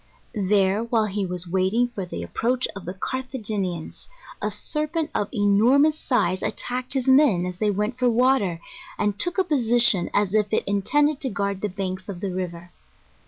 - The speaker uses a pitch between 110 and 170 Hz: No, high, 210 Hz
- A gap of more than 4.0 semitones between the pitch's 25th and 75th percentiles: Yes, average, 5.1 semitones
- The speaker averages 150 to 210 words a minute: Yes, average, 180 wpm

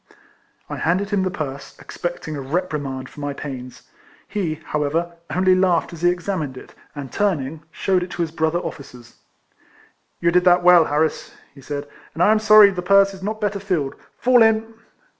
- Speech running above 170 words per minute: Yes, average, 185 wpm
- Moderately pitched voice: Yes, medium, 175 Hz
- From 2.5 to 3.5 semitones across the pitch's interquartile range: No, average, 4.5 semitones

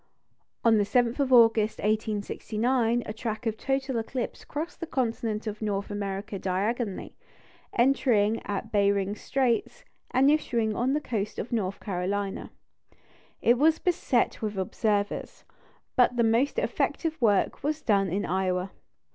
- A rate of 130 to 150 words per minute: Yes, average, 140 wpm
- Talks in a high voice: Yes, high, 225 Hz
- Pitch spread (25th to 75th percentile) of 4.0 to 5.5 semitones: No, average, 3.6 semitones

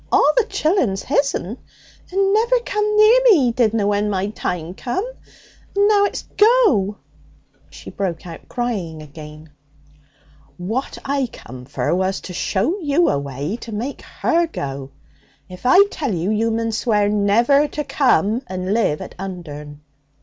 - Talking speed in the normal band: Yes, average, 155 wpm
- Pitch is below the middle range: No, high, 215 Hz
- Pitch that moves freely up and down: Yes, wide, 8.3 semitones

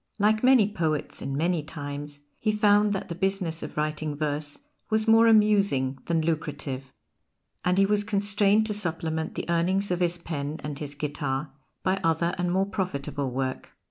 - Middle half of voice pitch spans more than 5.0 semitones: Yes, wide, 5.4 semitones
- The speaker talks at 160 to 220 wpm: Yes, average, 170 wpm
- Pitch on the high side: No, medium, 170 Hz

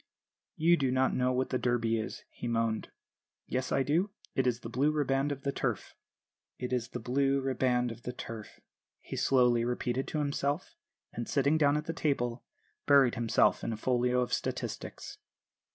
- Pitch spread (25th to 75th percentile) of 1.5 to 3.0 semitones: Yes, narrow, 2.6 semitones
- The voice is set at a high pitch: No, low, 130 Hz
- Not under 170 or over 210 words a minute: Yes, average, 180 wpm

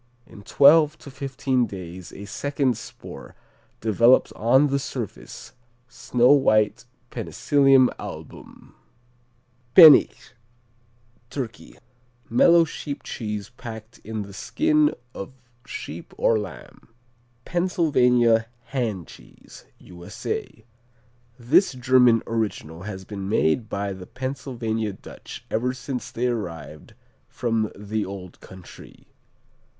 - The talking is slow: Yes, slow, 105 wpm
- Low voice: Yes, low, 115 Hz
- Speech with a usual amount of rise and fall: Yes, average, 4.4 semitones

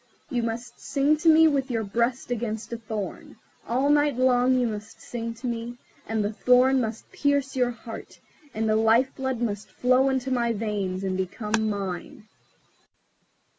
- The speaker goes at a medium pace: Yes, average, 170 wpm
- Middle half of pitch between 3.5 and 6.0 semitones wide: No, average, 3.0 semitones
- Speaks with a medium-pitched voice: No, high, 235 Hz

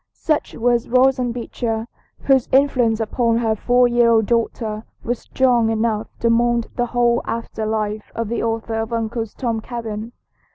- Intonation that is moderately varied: No, narrow, 1.5 semitones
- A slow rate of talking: No, average, 160 wpm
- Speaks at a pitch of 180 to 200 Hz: No, high, 230 Hz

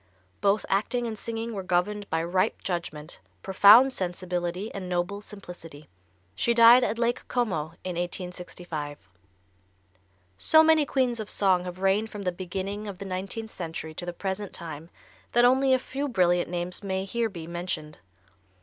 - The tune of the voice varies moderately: Yes, average, 4.1 semitones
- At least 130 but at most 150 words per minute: No, average, 160 wpm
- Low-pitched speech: No, high, 190 Hz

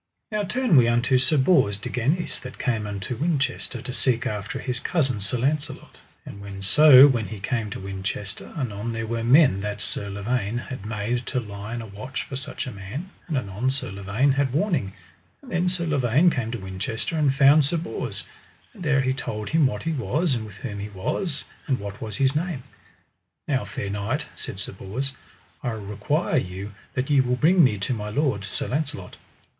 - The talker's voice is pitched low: Yes, low, 125 Hz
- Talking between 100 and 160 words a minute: No, average, 200 wpm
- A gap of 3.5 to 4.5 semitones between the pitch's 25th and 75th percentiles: No, wide, 5.6 semitones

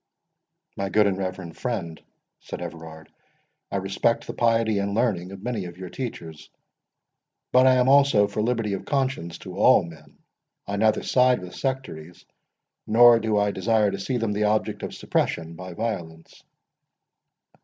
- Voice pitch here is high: No, low, 105 Hz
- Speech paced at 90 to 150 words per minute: No, average, 160 wpm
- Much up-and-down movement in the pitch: No, average, 4.5 semitones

